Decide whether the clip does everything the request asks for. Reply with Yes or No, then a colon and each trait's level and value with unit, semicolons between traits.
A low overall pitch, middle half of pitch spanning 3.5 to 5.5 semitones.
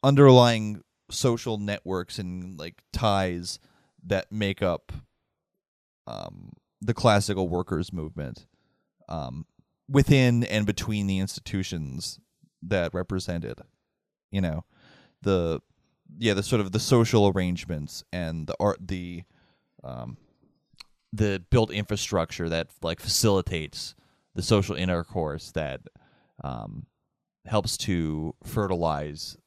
Yes: very low, 95 Hz; average, 3.9 semitones